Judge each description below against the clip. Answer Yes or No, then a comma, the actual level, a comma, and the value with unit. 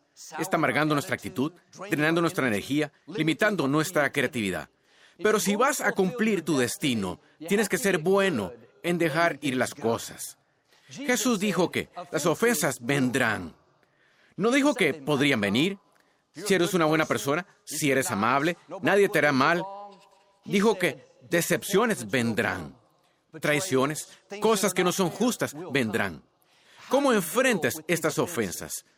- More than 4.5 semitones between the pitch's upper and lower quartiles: Yes, average, 5.2 semitones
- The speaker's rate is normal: Yes, average, 135 wpm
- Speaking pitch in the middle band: Yes, medium, 170 Hz